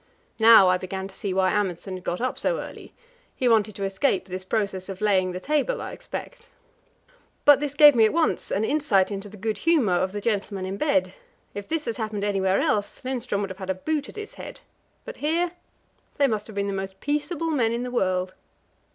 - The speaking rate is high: Yes, fast, 220 wpm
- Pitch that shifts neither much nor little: No, wide, 6.8 semitones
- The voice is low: No, high, 210 Hz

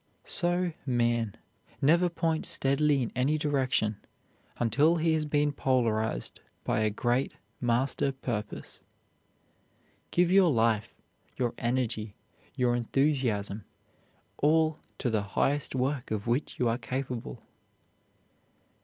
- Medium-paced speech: No, slow, 110 wpm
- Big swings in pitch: No, average, 4.3 semitones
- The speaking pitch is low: Yes, low, 130 Hz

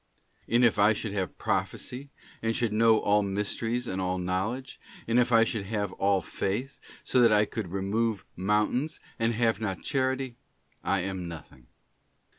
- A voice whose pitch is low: Yes, low, 105 Hz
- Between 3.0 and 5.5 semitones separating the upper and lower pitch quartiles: Yes, average, 3.3 semitones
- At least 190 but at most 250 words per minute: No, average, 165 wpm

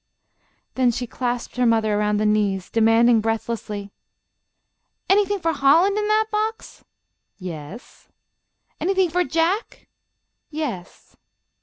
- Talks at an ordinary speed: No, slow, 110 wpm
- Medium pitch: No, high, 245 Hz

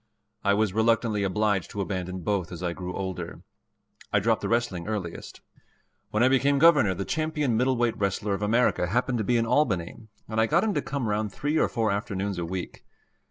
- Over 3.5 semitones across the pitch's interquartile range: Yes, average, 4.2 semitones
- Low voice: Yes, low, 105 Hz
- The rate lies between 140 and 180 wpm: No, average, 200 wpm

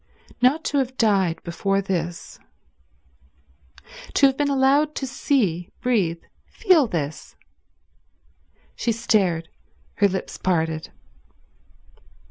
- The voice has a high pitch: Yes, high, 205 Hz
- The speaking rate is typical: No, slow, 100 wpm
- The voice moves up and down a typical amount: No, wide, 7.7 semitones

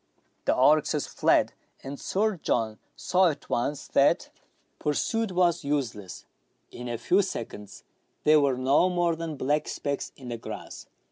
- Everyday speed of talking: Yes, average, 145 wpm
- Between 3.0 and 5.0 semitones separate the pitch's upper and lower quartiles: No, wide, 5.4 semitones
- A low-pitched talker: No, medium, 145 Hz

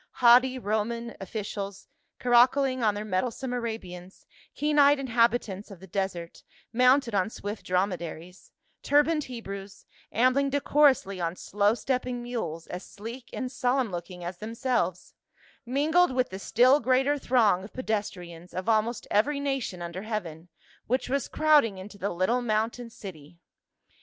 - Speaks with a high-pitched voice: Yes, high, 225 Hz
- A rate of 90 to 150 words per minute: Yes, average, 140 wpm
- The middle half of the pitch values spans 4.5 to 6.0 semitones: Yes, average, 5.1 semitones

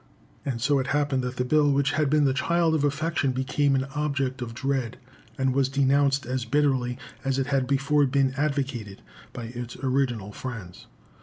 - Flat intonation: Yes, narrow, 2.1 semitones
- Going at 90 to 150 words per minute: No, average, 180 wpm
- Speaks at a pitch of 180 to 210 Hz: No, low, 135 Hz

